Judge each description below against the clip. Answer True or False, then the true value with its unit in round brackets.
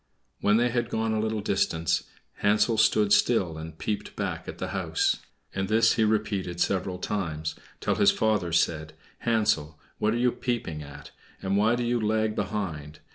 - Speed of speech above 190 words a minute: False (175 wpm)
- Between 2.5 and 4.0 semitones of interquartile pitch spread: False (4.5 semitones)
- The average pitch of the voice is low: True (105 Hz)